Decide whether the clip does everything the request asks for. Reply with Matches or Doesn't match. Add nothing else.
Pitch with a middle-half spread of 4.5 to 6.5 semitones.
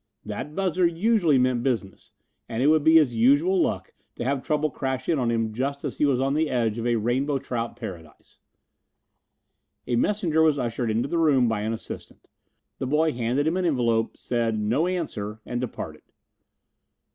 Matches